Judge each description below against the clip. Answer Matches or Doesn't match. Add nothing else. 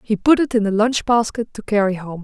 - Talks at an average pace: Doesn't match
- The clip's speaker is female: Matches